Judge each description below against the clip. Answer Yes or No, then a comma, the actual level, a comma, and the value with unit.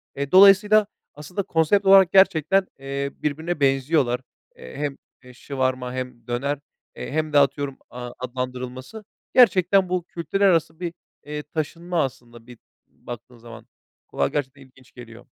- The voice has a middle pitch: Yes, medium, 145 Hz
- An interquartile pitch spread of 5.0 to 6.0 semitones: Yes, wide, 5.6 semitones